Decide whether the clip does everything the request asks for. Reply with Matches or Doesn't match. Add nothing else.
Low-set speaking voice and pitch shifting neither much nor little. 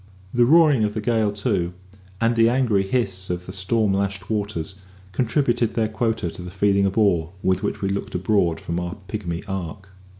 Matches